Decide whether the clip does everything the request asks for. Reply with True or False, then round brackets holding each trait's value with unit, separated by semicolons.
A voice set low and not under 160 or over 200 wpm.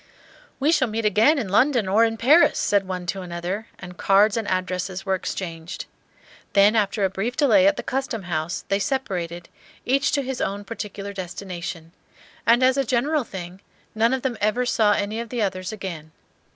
False (205 Hz; 185 wpm)